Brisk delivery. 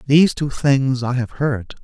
No: average, 195 wpm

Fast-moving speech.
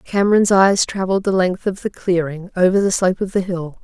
Yes: fast, 220 wpm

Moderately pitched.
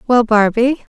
No: high, 235 Hz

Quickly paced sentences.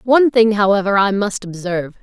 No: average, 180 wpm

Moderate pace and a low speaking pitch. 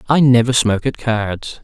Yes: average, 185 wpm; low, 120 Hz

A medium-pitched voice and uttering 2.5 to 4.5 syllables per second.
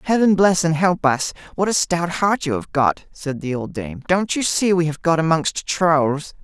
Yes: medium, 165 Hz; 4.4 syllables/s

